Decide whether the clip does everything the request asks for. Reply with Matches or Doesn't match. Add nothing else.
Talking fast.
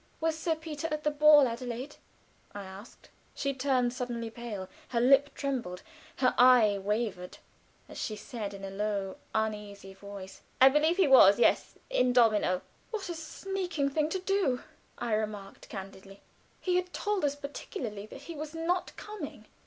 Doesn't match